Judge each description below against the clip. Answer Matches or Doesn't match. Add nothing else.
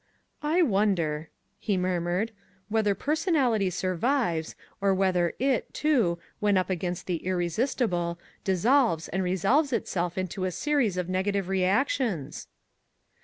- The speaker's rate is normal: Doesn't match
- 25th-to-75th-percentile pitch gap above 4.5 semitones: Matches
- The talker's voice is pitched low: Doesn't match